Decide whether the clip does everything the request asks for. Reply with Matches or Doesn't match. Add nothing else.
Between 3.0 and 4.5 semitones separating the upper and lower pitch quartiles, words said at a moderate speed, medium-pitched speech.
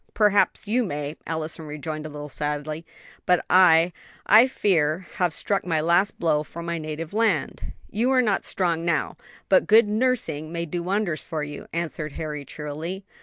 Matches